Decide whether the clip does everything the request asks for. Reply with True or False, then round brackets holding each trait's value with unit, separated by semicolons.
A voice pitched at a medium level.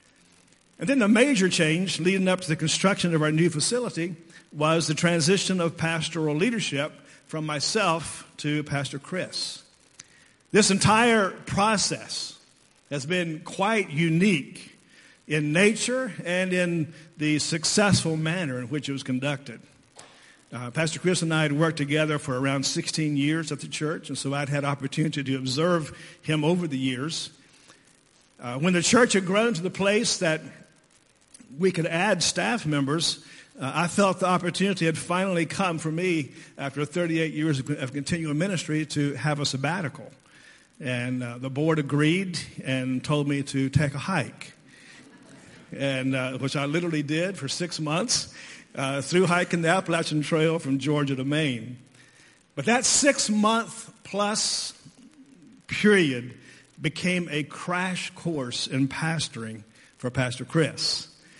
True (160 Hz)